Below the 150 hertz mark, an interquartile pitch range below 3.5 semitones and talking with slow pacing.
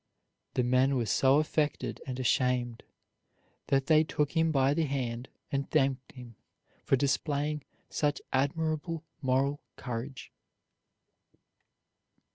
Yes: low, 135 Hz; narrow, 2.6 semitones; slow, 115 wpm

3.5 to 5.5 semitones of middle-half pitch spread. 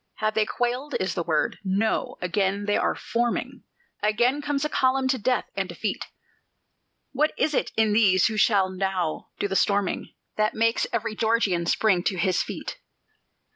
Yes: average, 4.0 semitones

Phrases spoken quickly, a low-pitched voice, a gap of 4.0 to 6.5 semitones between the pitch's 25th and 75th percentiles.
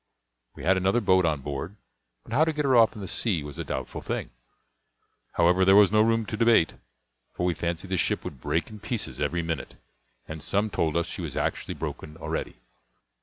Yes: fast, 210 wpm; very low, 95 Hz; average, 4.9 semitones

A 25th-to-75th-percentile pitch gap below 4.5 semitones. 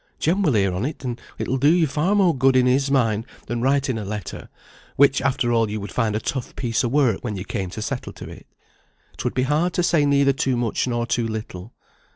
Yes: average, 4.1 semitones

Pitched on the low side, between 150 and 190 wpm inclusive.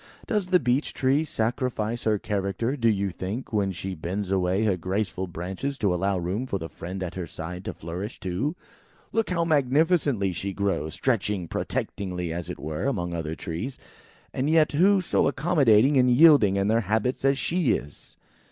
Yes: low, 105 Hz; average, 180 wpm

